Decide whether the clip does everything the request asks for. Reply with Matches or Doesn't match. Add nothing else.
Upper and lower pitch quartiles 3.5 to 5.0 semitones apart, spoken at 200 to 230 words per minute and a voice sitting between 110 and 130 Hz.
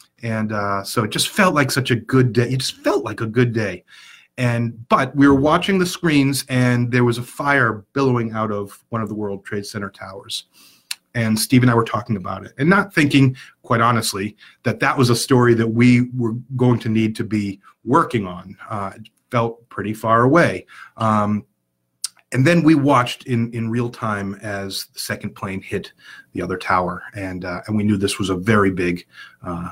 Matches